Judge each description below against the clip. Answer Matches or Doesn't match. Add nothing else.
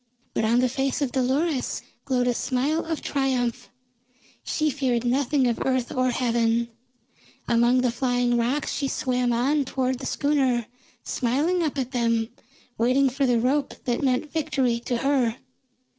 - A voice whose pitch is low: Doesn't match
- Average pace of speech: Matches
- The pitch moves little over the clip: Matches